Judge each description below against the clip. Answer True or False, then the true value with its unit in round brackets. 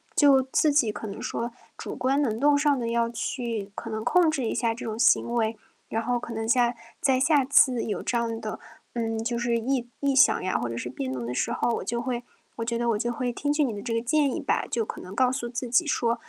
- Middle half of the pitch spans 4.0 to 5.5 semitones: False (2.7 semitones)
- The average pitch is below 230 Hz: False (235 Hz)